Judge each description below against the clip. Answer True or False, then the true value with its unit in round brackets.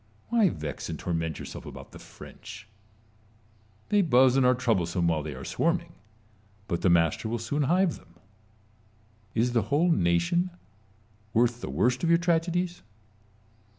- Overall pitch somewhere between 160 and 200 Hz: False (120 Hz)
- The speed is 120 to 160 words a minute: True (150 wpm)